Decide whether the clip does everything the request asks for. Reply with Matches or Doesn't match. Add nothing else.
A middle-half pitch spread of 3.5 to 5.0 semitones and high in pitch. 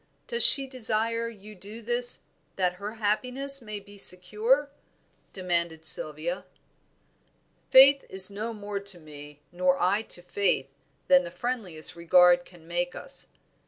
Matches